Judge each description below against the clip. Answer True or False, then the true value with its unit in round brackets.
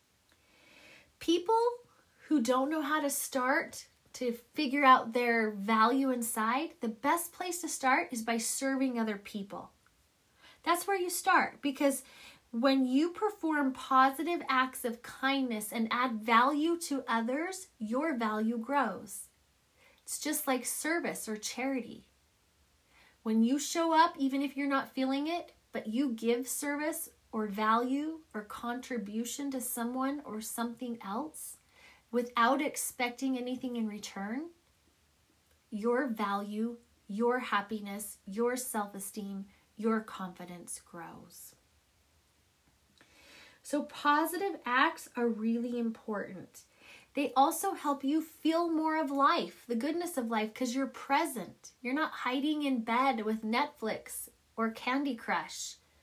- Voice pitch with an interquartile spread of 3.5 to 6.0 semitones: True (4.0 semitones)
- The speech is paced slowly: True (125 wpm)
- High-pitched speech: True (255 Hz)